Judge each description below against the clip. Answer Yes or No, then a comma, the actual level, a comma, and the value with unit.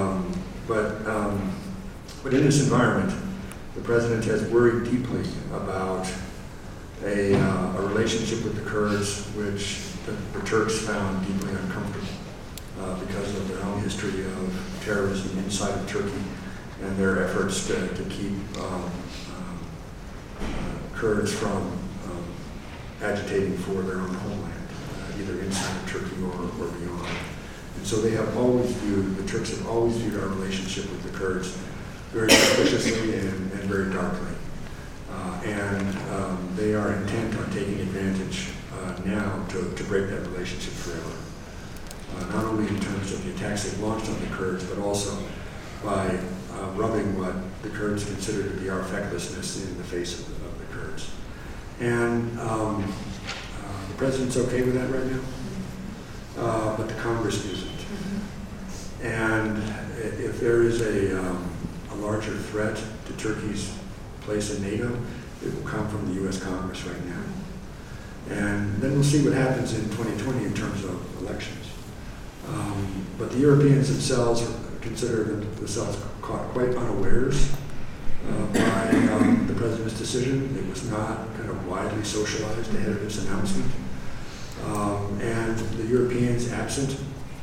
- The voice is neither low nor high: No, low, 100 Hz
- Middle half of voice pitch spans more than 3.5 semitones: No, average, 2.7 semitones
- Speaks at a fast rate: No, average, 150 wpm